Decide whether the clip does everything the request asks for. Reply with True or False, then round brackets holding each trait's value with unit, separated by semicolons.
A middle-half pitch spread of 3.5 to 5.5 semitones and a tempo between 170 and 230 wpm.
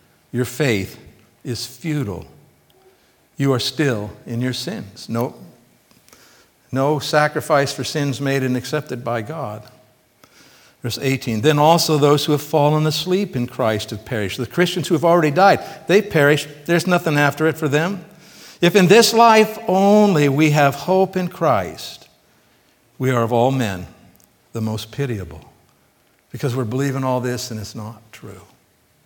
False (4.9 semitones; 155 wpm)